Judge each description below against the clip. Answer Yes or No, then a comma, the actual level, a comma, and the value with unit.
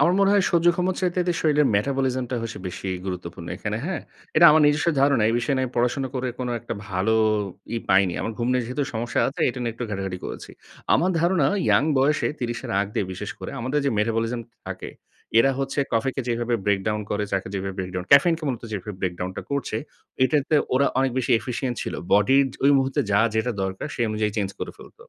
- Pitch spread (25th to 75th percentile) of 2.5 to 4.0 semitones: No, average, 5.0 semitones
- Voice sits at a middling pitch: No, low, 120 Hz